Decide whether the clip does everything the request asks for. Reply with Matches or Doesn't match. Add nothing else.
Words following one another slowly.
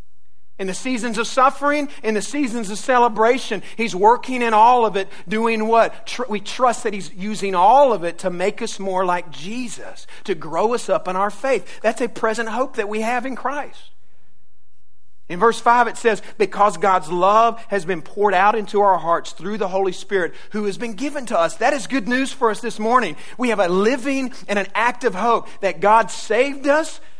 Doesn't match